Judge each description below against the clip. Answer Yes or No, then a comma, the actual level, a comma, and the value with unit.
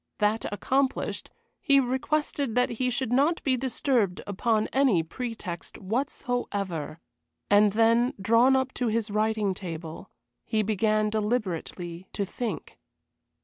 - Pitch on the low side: No, high, 220 Hz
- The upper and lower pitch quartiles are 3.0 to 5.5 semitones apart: Yes, average, 3.9 semitones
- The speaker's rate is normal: No, slow, 120 wpm